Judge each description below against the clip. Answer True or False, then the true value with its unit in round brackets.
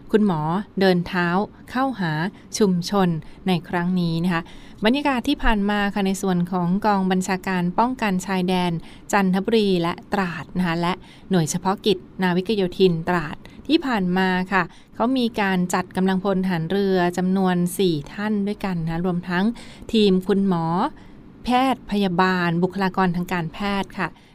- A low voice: False (190 Hz)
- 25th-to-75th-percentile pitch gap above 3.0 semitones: False (2.4 semitones)